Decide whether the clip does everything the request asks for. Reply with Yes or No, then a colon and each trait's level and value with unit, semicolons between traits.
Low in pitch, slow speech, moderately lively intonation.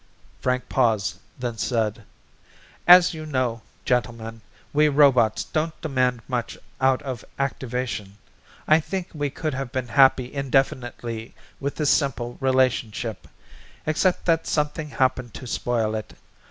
Yes: low, 130 Hz; slow, 125 wpm; average, 3.5 semitones